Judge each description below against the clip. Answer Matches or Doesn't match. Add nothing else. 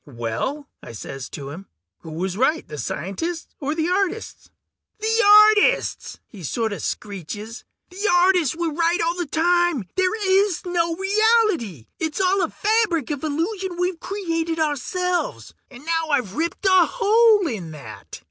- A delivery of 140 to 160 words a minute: Matches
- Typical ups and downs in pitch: Doesn't match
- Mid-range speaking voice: Doesn't match